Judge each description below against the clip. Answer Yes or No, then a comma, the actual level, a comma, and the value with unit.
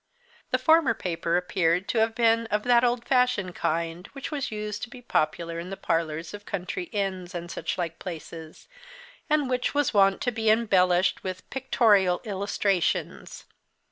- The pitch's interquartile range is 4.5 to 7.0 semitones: Yes, average, 4.8 semitones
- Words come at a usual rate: Yes, average, 160 wpm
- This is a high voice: Yes, high, 195 Hz